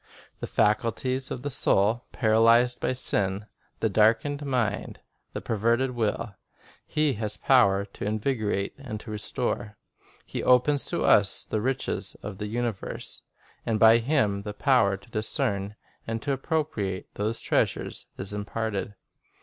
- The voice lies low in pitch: Yes, low, 110 Hz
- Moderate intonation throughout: Yes, average, 3.4 semitones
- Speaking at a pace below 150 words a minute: Yes, average, 140 wpm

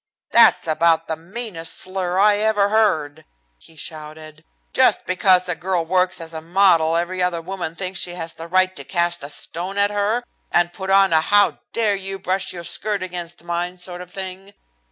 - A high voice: No, medium, 180 Hz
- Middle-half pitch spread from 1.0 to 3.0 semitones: Yes, narrow, 2.6 semitones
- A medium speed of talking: Yes, average, 190 wpm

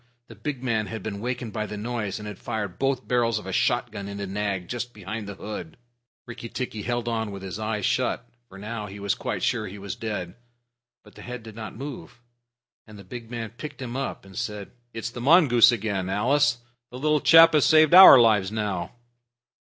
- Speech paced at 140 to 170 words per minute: No, fast, 205 wpm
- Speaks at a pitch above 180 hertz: No, low, 110 Hz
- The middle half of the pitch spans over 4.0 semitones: No, average, 3.2 semitones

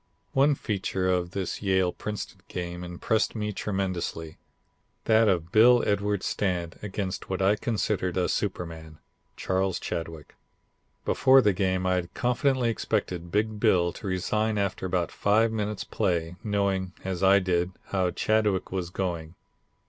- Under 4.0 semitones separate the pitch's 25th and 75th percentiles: Yes, average, 2.9 semitones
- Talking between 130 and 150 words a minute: Yes, average, 140 wpm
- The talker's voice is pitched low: Yes, very low, 95 Hz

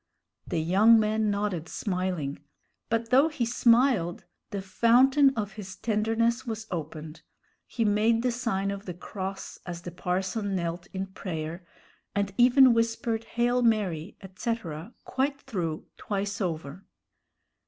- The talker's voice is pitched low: No, high, 205 Hz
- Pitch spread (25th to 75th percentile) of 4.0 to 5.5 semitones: Yes, average, 4.3 semitones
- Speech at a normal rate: No, slow, 130 wpm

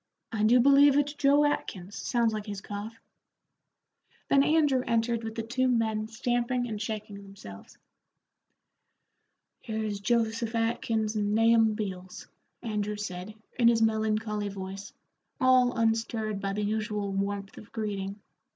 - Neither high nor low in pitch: No, high, 220 Hz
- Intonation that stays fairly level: Yes, narrow, 2.3 semitones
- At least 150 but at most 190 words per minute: No, slow, 135 wpm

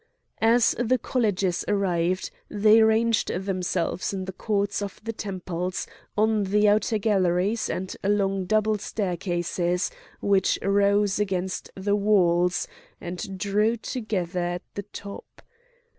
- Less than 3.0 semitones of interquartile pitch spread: Yes, narrow, 2.6 semitones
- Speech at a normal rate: No, slow, 120 wpm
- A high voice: Yes, high, 200 Hz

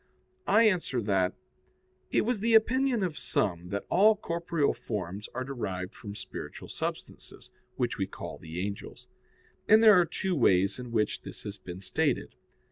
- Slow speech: No, average, 160 wpm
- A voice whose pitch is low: Yes, low, 125 Hz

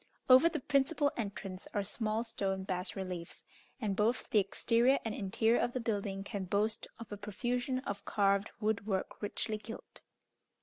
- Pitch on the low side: No, high, 210 Hz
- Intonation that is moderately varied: Yes, average, 3.3 semitones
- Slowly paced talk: No, average, 165 wpm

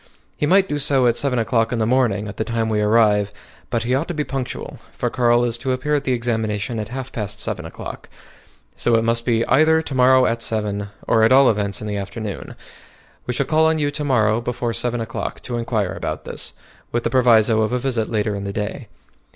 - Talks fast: Yes, fast, 230 wpm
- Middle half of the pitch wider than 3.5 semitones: No, average, 3.1 semitones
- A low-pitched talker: Yes, low, 115 Hz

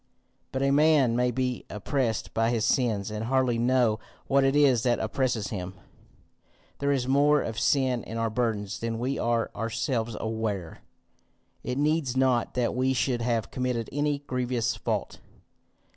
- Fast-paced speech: No, average, 160 wpm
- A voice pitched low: Yes, low, 125 Hz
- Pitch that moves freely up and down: No, average, 2.7 semitones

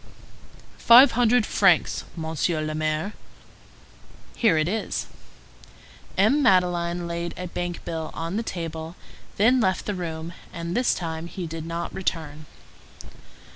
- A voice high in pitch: No, medium, 170 Hz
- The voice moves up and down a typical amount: Yes, average, 3.2 semitones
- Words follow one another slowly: Yes, slow, 130 wpm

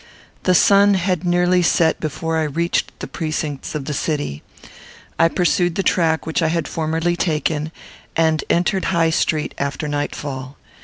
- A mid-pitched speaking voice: Yes, medium, 160 Hz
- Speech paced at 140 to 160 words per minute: Yes, average, 155 wpm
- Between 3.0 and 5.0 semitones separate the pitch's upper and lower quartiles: No, narrow, 2.4 semitones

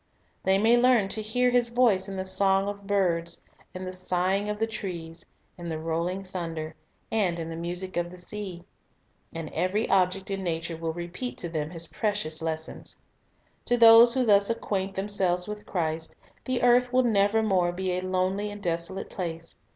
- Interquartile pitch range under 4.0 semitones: Yes, average, 3.4 semitones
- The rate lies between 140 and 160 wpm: No, average, 180 wpm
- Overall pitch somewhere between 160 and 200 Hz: Yes, high, 190 Hz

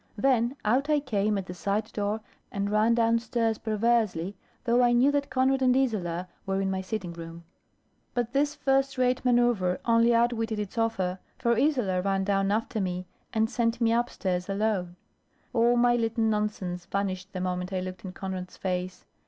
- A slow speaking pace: No, average, 175 wpm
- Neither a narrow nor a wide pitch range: Yes, average, 4.2 semitones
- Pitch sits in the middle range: No, high, 220 Hz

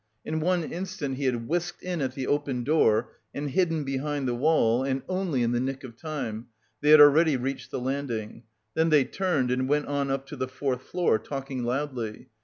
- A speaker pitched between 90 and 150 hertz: Yes, low, 135 Hz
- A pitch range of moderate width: Yes, average, 3.3 semitones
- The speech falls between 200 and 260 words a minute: Yes, fast, 205 wpm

